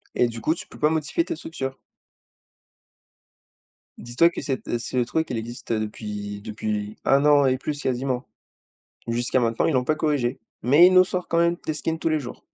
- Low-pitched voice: Yes, low, 130 Hz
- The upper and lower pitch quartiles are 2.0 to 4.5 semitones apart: No, average, 5.0 semitones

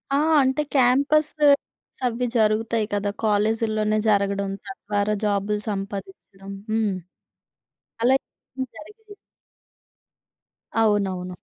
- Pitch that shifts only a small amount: No, average, 3.7 semitones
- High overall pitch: Yes, high, 215 Hz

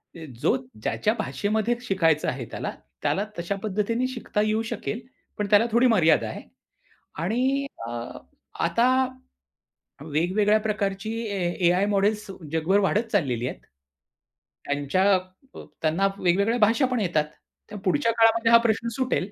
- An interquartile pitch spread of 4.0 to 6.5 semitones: Yes, average, 4.4 semitones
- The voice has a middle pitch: No, high, 205 Hz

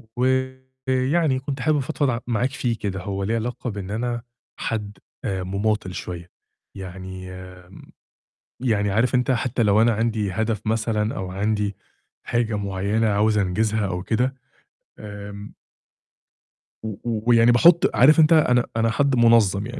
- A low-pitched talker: Yes, low, 110 Hz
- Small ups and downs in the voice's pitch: No, average, 3.7 semitones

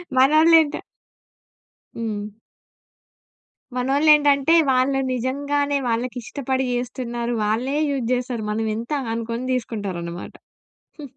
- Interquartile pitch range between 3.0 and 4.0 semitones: Yes, average, 3.4 semitones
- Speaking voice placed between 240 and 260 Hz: Yes, very high, 255 Hz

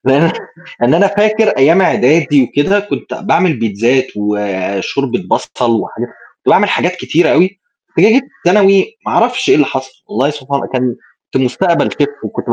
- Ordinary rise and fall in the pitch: No, wide, 7.5 semitones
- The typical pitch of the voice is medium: Yes, medium, 145 Hz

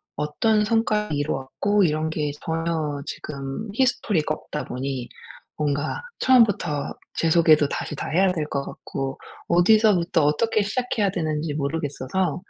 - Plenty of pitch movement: Yes, wide, 5.7 semitones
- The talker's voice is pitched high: No, medium, 160 Hz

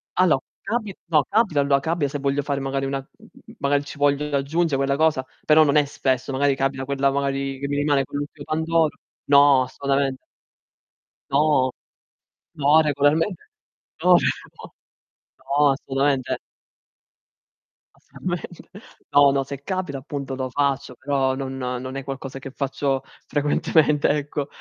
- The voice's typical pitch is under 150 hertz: Yes, medium, 140 Hz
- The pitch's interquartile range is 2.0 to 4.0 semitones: No, narrow, 1.5 semitones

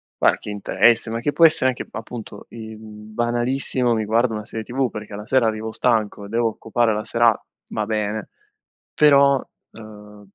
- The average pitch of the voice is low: Yes, low, 110 Hz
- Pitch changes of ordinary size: No, narrow, 2.0 semitones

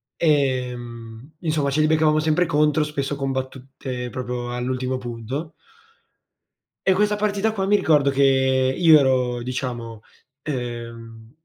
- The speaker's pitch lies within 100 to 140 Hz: Yes, low, 135 Hz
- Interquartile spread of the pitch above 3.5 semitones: Yes, average, 3.9 semitones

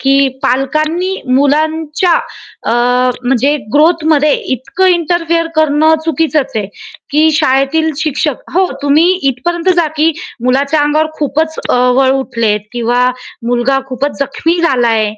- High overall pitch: Yes, very high, 295 Hz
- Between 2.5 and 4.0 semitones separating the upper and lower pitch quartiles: Yes, average, 3.3 semitones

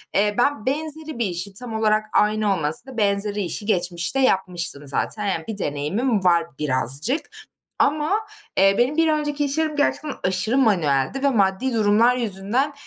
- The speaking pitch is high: Yes, high, 210 Hz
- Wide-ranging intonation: Yes, wide, 6.2 semitones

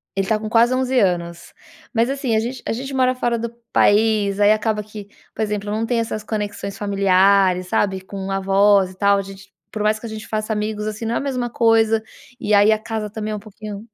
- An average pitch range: No, narrow, 2.1 semitones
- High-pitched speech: Yes, high, 215 Hz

